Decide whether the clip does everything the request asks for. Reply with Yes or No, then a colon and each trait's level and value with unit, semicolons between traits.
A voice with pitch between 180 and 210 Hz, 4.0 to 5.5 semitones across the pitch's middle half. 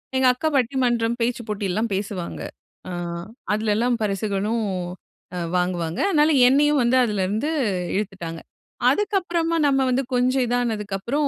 No: high, 235 Hz; average, 4.5 semitones